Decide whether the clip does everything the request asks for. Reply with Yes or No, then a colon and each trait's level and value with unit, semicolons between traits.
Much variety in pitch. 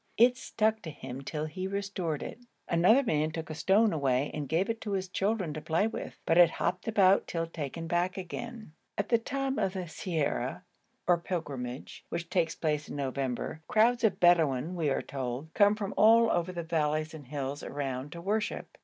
No: average, 5.0 semitones